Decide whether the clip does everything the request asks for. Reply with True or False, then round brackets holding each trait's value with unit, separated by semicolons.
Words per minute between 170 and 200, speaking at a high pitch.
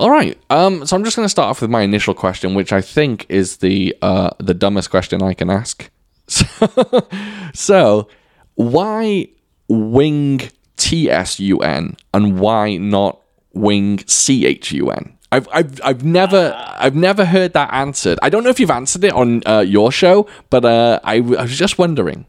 False (180 wpm; 125 Hz)